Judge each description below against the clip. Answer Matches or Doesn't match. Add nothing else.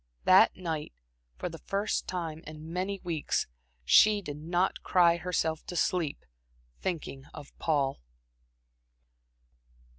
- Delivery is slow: Matches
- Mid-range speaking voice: Matches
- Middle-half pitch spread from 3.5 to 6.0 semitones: Doesn't match